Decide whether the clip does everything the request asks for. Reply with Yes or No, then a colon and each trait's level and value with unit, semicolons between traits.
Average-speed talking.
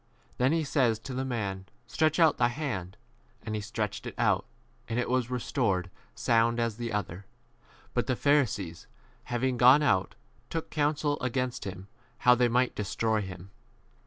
Yes: average, 165 wpm